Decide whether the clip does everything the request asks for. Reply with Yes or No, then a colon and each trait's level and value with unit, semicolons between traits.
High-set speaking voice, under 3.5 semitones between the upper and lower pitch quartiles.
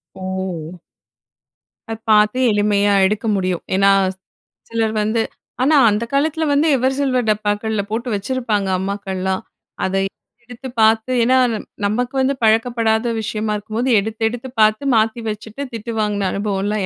Yes: high, 215 Hz; average, 2.9 semitones